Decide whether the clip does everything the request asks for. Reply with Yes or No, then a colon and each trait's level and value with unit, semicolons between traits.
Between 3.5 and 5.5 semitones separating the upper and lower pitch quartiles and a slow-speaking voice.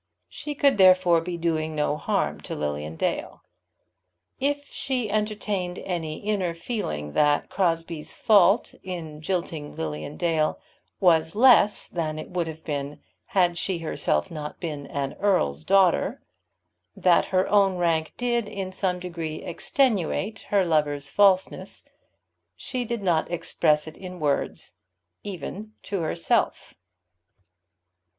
Yes: average, 4.3 semitones; slow, 130 wpm